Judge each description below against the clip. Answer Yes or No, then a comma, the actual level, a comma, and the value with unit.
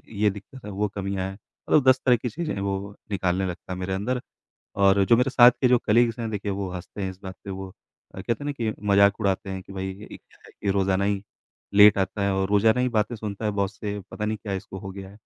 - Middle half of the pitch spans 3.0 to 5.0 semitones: No, narrow, 2.4 semitones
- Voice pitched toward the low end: Yes, low, 100 Hz